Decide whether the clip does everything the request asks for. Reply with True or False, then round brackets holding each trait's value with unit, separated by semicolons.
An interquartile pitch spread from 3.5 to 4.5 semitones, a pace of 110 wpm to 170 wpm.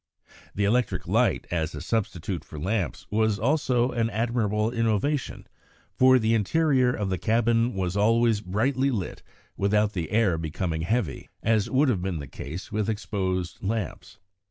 True (4.1 semitones; 155 wpm)